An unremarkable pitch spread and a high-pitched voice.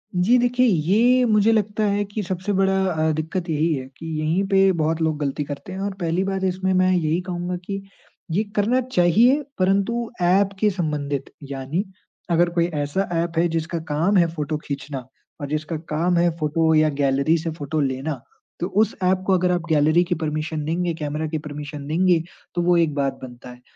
No: average, 3.8 semitones; medium, 170 Hz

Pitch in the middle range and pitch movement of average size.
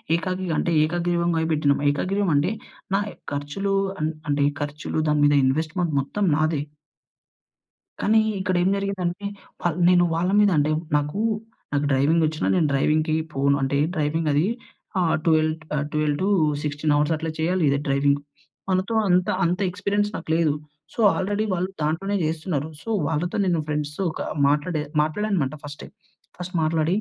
Yes: medium, 160 Hz; average, 3.6 semitones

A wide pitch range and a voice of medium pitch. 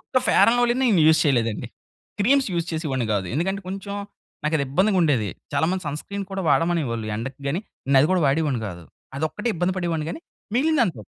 Yes: wide, 6.2 semitones; medium, 160 Hz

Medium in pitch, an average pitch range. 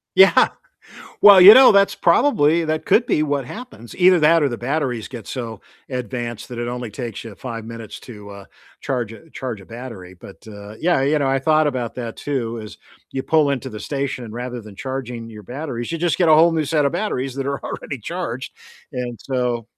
No: low, 130 Hz; average, 5.0 semitones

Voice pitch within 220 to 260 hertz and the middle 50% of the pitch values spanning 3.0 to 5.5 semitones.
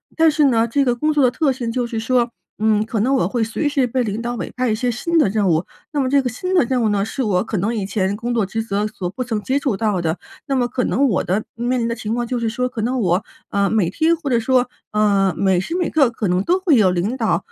Yes: high, 235 Hz; average, 3.7 semitones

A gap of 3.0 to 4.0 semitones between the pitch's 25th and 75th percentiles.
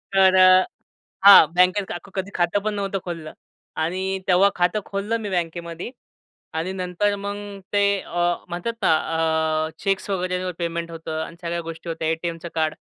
No: narrow, 2.6 semitones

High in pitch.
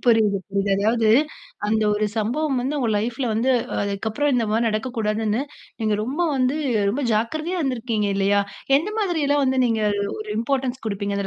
Yes: high, 230 Hz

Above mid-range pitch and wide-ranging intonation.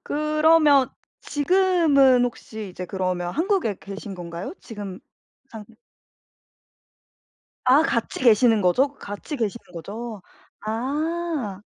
Yes: high, 240 Hz; wide, 7.1 semitones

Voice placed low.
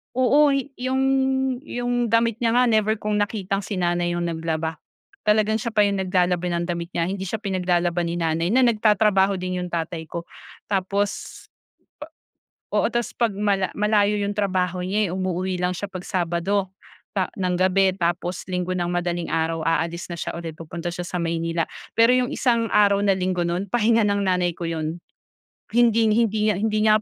No: high, 190 Hz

